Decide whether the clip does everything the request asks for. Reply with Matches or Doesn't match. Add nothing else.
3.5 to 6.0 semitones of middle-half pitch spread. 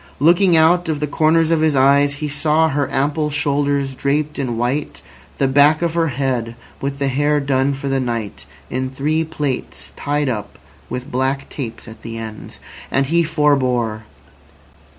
Doesn't match